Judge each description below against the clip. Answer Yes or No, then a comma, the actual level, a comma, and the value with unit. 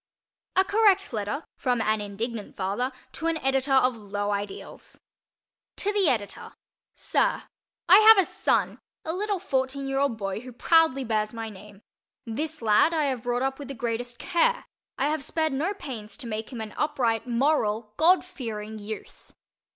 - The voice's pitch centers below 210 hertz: No, very high, 255 Hz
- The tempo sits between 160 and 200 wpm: Yes, average, 165 wpm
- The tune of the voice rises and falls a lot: Yes, wide, 6.2 semitones